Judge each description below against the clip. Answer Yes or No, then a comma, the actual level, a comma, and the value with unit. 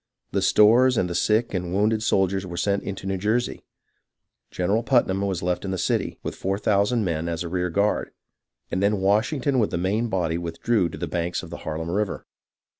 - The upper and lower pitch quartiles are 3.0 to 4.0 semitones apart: Yes, average, 3.3 semitones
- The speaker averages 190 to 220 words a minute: Yes, average, 200 wpm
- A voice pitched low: Yes, very low, 95 Hz